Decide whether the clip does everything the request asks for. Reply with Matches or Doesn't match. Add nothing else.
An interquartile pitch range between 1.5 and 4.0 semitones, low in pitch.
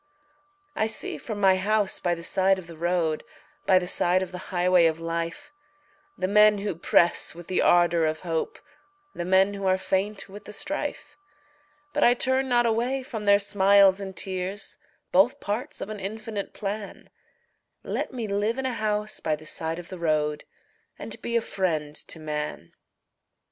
Doesn't match